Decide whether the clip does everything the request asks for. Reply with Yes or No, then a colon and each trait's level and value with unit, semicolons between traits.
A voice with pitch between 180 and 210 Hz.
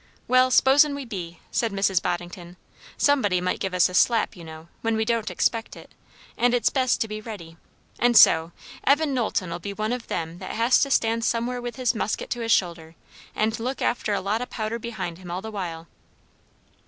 No: high, 220 Hz